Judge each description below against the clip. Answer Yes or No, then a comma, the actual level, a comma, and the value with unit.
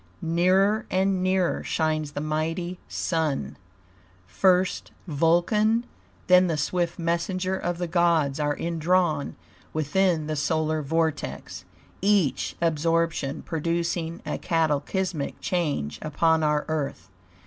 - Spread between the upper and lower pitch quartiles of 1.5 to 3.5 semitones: Yes, average, 2.9 semitones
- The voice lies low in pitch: No, medium, 165 Hz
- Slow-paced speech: Yes, slow, 105 wpm